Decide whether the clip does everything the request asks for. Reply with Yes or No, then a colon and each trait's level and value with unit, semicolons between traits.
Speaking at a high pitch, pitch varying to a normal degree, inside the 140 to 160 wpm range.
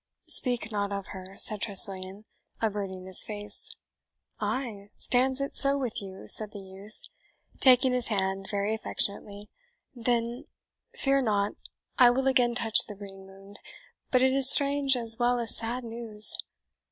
Yes: high, 220 Hz; average, 3.8 semitones; average, 150 wpm